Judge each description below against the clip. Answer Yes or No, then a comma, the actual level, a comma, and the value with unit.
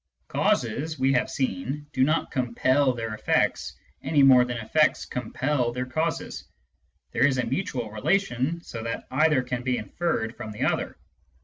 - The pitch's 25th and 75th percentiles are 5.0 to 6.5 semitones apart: No, average, 3.5 semitones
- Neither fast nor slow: Yes, average, 155 wpm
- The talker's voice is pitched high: No, low, 130 Hz